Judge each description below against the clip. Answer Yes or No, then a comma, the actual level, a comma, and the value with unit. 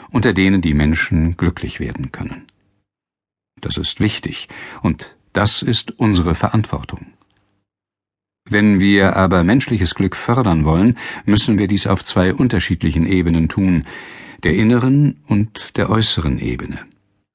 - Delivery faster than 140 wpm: No, slow, 125 wpm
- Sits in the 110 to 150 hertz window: No, low, 100 Hz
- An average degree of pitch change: Yes, average, 3.5 semitones